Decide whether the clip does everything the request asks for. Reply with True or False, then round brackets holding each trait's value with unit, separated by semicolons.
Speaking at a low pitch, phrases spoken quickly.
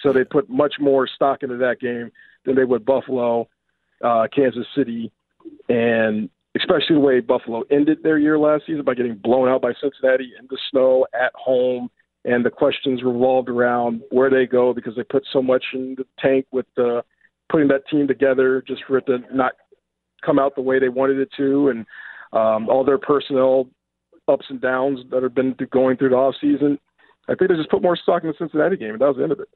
True (130 Hz; 215 wpm)